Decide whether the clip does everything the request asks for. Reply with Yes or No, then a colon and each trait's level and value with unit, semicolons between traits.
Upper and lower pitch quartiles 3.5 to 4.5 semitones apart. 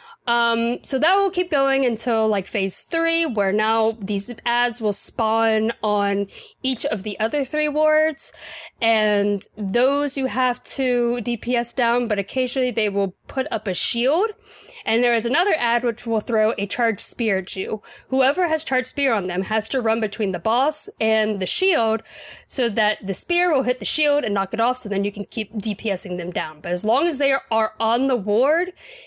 Yes: average, 4.0 semitones